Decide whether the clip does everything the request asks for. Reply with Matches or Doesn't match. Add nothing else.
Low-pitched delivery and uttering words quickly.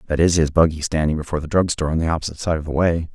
Matches